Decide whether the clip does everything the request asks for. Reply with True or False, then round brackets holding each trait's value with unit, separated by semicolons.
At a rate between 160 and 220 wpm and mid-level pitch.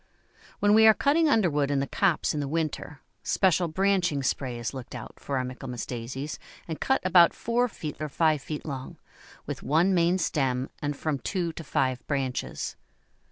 True (180 wpm; 155 Hz)